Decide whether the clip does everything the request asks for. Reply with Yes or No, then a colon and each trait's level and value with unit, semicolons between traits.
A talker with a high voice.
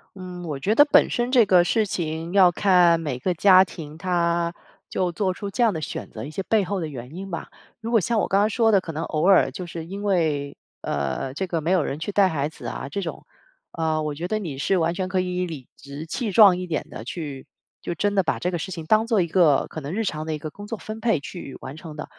No: medium, 175 Hz